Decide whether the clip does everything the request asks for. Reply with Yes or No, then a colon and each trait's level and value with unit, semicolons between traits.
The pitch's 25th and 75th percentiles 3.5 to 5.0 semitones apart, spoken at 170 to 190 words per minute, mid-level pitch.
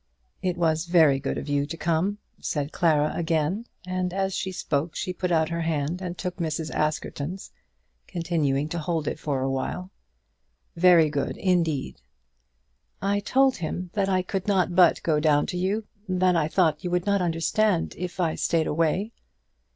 No: average, 3.0 semitones; average, 175 wpm; medium, 170 Hz